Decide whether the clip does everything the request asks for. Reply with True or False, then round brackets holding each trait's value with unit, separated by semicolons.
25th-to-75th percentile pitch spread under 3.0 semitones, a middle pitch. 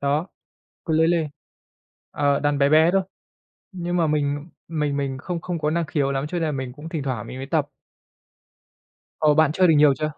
True (2.6 semitones; 150 Hz)